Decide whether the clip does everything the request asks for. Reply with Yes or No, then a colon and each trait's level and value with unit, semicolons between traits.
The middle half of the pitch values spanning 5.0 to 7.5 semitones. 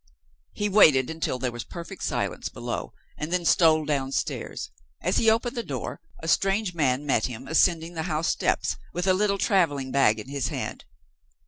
Yes: wide, 5.4 semitones